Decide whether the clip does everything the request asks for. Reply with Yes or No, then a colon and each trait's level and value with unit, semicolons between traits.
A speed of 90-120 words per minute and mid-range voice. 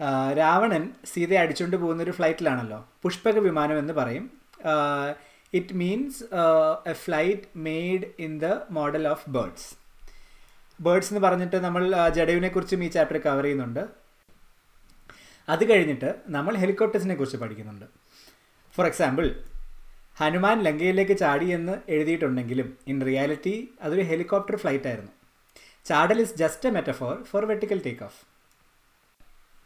Yes: average, 115 wpm; medium, 170 Hz